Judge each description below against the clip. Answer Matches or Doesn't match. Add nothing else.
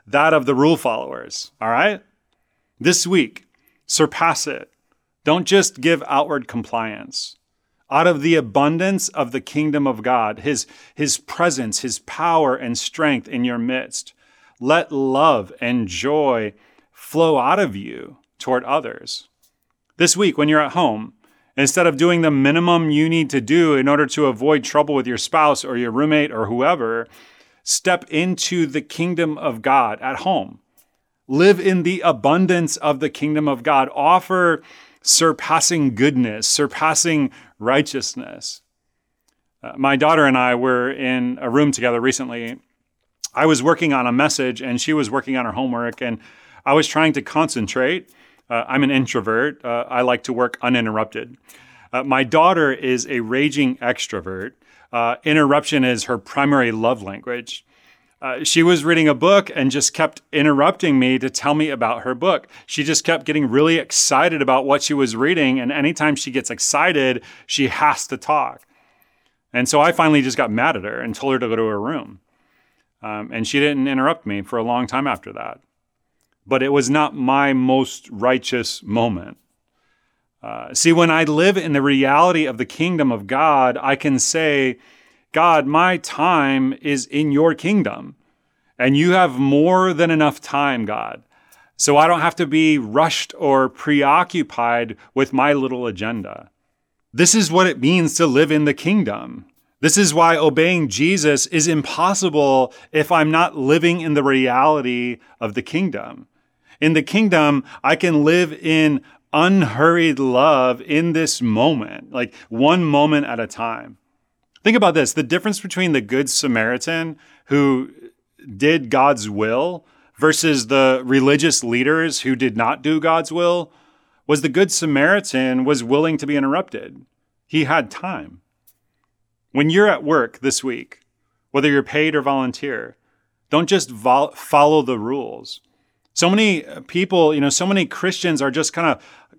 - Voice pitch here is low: Doesn't match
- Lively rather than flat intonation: Doesn't match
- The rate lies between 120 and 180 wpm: Matches